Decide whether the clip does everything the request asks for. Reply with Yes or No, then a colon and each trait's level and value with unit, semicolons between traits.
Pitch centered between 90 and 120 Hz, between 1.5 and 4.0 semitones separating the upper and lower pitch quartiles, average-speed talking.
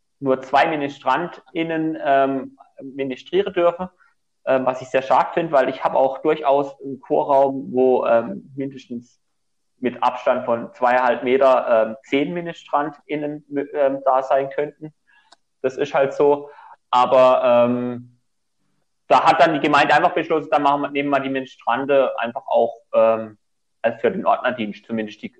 No: low, 135 Hz; narrow, 2.6 semitones; average, 150 wpm